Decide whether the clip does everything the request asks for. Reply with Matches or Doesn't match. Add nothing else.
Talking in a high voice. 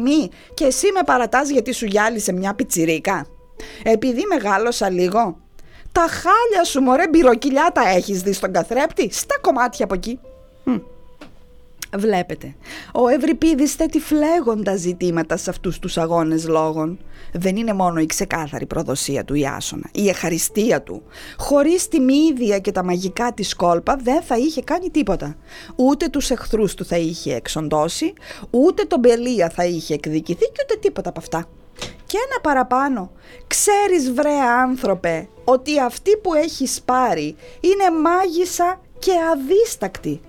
Matches